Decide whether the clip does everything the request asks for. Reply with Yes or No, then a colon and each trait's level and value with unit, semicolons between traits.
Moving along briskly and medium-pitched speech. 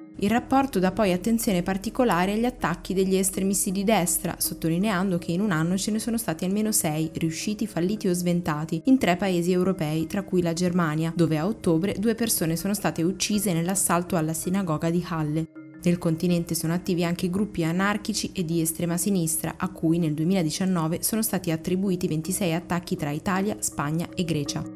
Yes: fast, 175 wpm; medium, 180 Hz